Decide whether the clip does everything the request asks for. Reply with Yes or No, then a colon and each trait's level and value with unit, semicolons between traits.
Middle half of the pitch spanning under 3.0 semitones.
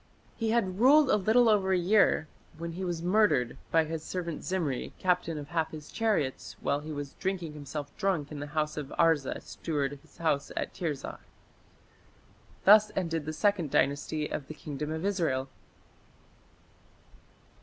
No: average, 4.3 semitones